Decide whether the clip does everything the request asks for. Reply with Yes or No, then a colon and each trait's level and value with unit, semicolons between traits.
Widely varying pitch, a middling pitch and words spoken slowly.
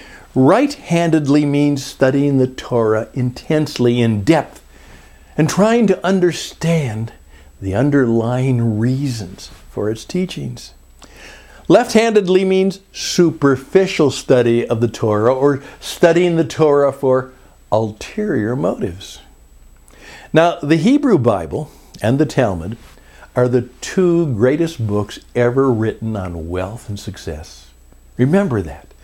No: wide, 7.1 semitones; low, 130 Hz; slow, 105 wpm